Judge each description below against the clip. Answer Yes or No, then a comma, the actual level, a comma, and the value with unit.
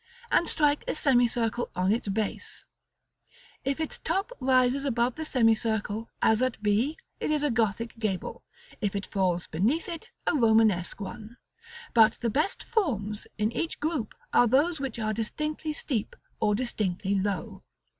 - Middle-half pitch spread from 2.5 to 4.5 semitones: No, average, 5.0 semitones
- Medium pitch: No, high, 230 Hz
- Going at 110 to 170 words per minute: Yes, average, 155 wpm